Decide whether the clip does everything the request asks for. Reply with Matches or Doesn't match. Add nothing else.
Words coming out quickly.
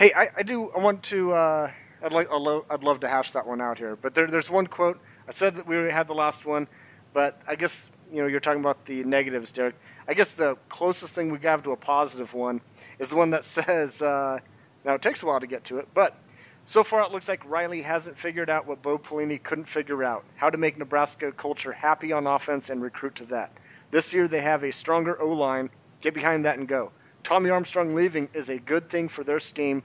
Matches